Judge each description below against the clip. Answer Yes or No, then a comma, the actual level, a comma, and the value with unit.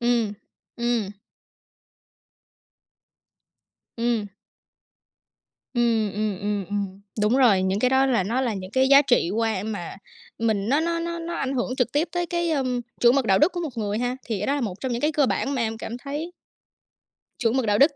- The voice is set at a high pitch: Yes, high, 240 Hz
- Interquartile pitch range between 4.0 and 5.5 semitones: Yes, average, 4.6 semitones